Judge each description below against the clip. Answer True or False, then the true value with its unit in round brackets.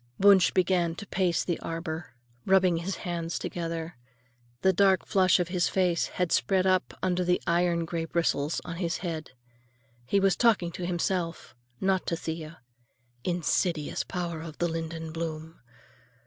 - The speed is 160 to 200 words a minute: False (150 wpm)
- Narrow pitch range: True (2.0 semitones)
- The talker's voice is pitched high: False (175 Hz)